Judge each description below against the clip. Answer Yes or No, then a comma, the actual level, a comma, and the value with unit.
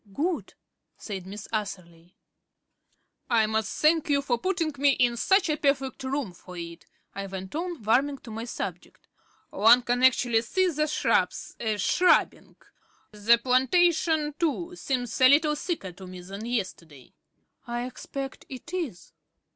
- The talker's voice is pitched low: No, high, 245 Hz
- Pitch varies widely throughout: Yes, wide, 6.3 semitones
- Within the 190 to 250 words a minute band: No, average, 145 wpm